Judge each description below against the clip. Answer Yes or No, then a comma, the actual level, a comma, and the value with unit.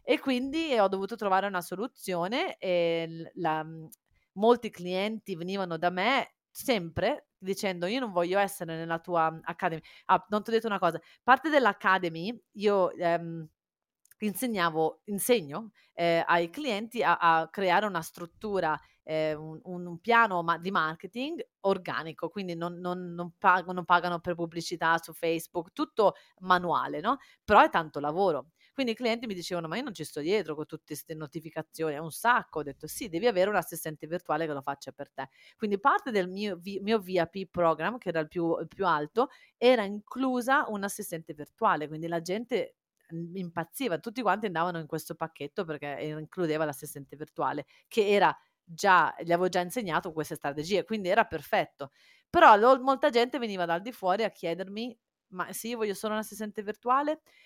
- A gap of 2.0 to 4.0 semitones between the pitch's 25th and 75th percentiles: No, average, 4.6 semitones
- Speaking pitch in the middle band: Yes, medium, 180 Hz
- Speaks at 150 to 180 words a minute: Yes, fast, 170 wpm